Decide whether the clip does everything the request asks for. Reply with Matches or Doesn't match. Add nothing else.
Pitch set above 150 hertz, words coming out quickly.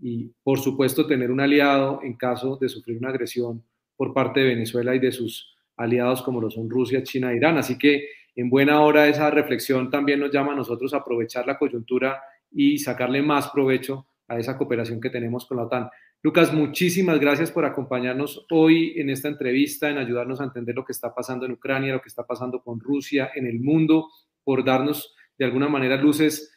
Doesn't match